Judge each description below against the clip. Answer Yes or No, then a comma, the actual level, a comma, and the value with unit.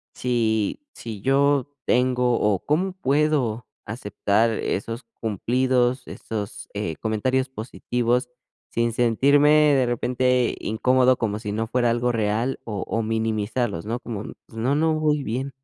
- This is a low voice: Yes, low, 120 Hz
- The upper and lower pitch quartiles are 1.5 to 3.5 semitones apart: Yes, average, 2.9 semitones